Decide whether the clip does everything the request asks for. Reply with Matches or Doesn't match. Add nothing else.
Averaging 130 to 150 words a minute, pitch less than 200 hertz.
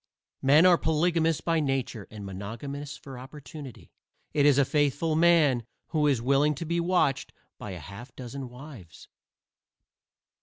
Matches